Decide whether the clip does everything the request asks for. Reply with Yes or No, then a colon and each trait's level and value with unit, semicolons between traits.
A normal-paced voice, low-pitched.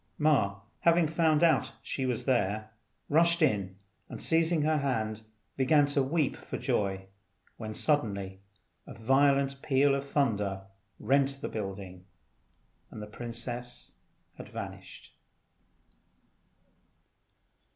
No: slow, 110 wpm; low, 130 Hz